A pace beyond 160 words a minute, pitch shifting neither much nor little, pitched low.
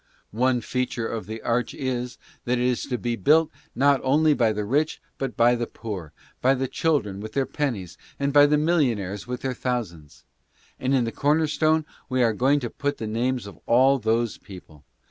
Yes: average, 200 wpm; average, 3.9 semitones; low, 125 Hz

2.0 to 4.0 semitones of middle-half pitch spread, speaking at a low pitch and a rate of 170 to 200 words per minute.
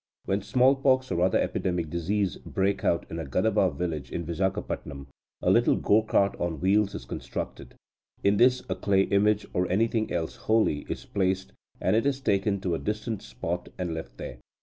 Yes: average, 3.7 semitones; very low, 95 Hz; average, 180 wpm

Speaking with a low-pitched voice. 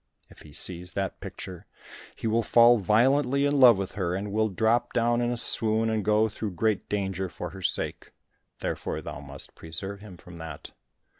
Yes: low, 105 Hz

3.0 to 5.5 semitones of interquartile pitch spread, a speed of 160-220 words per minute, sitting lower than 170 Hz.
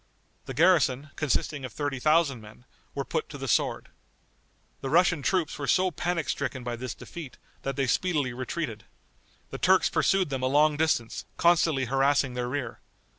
Yes: average, 3.9 semitones; average, 170 wpm; medium, 140 Hz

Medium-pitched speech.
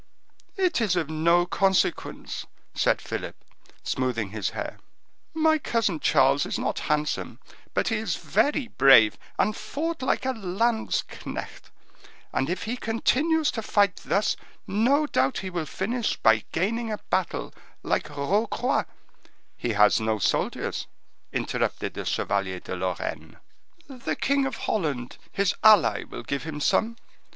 No: high, 195 Hz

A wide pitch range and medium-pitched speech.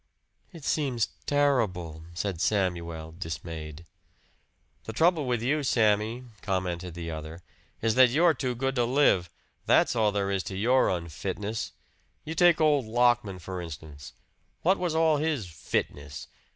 No: wide, 7.7 semitones; low, 105 Hz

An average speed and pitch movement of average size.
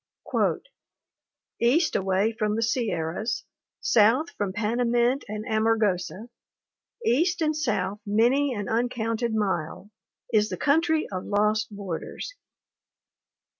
No: slow, 105 wpm; average, 3.0 semitones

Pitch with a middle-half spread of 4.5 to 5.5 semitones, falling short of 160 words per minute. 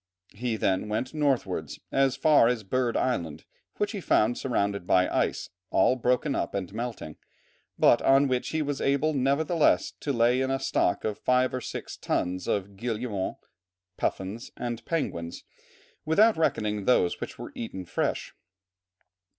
Yes: average, 5.1 semitones; average, 150 wpm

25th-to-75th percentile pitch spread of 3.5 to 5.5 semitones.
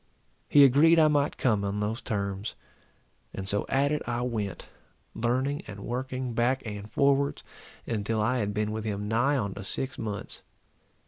Yes: average, 4.4 semitones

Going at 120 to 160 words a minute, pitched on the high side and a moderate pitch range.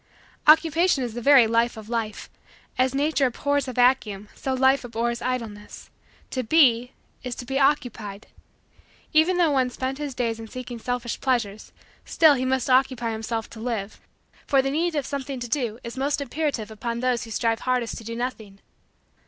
No: average, 175 wpm; very high, 250 Hz; average, 3.0 semitones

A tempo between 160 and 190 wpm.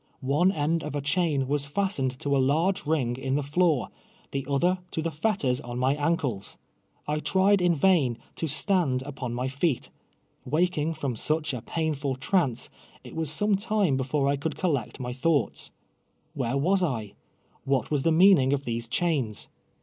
Yes: average, 175 wpm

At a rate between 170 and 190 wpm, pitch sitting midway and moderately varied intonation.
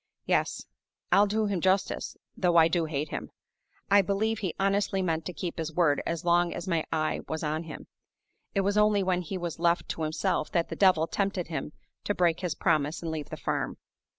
No: fast, 205 wpm; medium, 175 Hz; average, 3.3 semitones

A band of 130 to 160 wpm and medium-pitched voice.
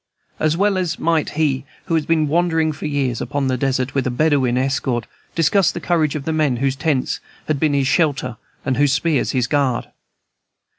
No: average, 190 wpm; medium, 145 Hz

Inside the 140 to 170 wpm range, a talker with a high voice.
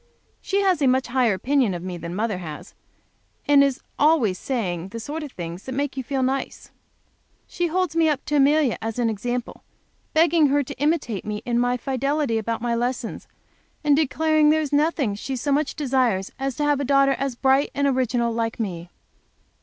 No: average, 195 wpm; very high, 265 Hz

